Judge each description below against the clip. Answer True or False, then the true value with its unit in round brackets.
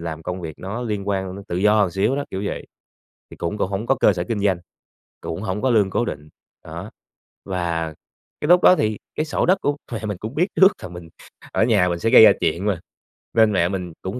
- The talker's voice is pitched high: False (100 Hz)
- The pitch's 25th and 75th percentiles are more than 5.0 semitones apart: False (4.0 semitones)